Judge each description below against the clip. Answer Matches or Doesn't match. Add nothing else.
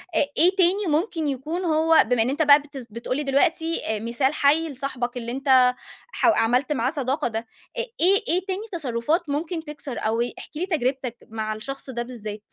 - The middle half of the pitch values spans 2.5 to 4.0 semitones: Doesn't match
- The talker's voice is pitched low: Doesn't match